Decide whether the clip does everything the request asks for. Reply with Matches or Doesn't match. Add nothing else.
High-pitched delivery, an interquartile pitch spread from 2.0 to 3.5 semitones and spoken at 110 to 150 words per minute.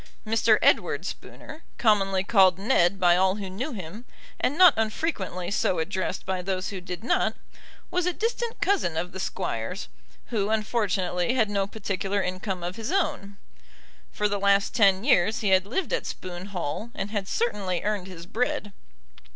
Doesn't match